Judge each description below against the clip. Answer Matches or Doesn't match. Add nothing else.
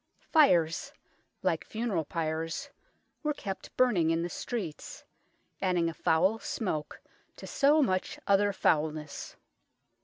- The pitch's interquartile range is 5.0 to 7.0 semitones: Matches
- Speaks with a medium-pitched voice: Matches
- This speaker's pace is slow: Matches